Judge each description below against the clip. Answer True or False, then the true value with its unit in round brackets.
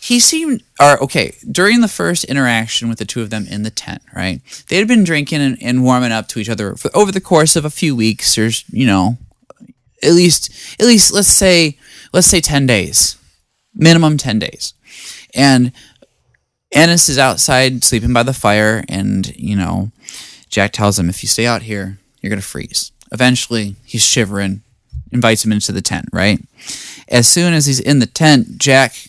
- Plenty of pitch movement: True (6.2 semitones)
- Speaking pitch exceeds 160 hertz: False (125 Hz)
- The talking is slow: False (190 wpm)